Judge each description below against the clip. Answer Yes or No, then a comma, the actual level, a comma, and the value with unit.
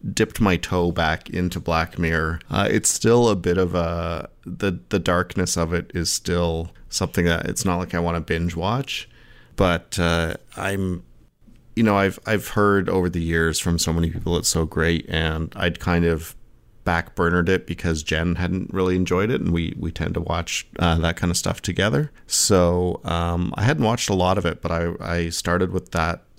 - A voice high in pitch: No, very low, 85 Hz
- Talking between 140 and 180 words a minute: No, average, 200 wpm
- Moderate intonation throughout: No, narrow, 1.9 semitones